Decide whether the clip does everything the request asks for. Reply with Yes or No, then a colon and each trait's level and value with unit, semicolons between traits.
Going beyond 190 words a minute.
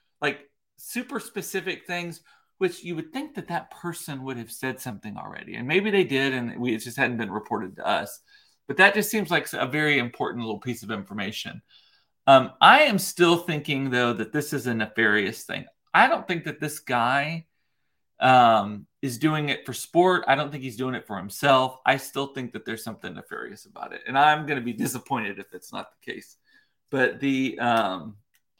Yes: average, 200 wpm